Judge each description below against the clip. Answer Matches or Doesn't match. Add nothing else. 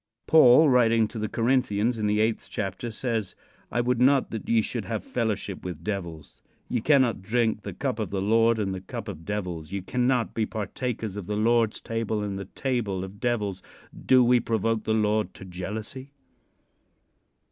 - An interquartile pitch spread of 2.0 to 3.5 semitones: Matches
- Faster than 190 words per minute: Doesn't match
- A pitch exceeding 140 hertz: Doesn't match